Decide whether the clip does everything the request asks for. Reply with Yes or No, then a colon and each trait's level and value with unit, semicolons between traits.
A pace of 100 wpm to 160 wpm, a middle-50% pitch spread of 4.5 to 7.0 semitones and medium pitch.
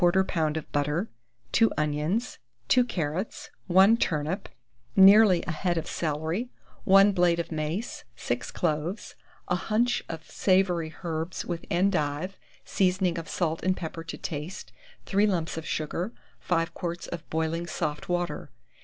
No: slow, 135 wpm; average, 3.2 semitones; medium, 175 Hz